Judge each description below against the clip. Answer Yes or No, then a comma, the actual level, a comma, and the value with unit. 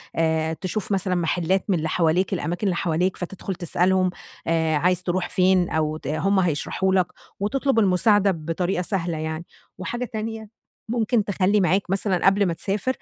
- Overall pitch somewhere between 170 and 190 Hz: Yes, medium, 185 Hz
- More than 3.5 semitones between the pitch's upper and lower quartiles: No, average, 2.7 semitones